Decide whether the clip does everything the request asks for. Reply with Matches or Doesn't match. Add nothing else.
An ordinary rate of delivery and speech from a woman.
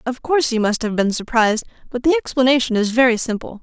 Doesn't match